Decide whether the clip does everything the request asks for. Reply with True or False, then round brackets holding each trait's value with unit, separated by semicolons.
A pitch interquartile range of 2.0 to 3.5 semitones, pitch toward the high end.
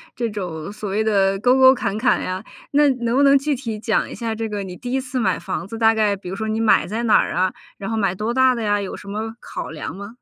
True (3.2 semitones; 220 Hz)